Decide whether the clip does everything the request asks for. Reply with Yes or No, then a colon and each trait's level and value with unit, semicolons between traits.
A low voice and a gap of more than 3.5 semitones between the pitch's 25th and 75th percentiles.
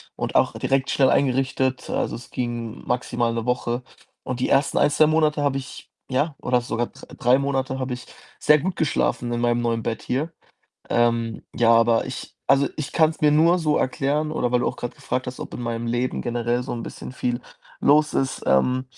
No: low, 130 Hz; average, 2.8 semitones